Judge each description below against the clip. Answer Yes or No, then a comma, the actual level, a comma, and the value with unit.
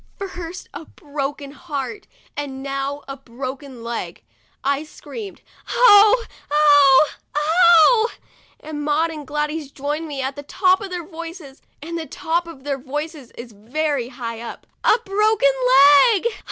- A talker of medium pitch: No, very high, 295 Hz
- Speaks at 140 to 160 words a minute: Yes, average, 145 wpm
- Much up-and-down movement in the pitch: No, average, 3.6 semitones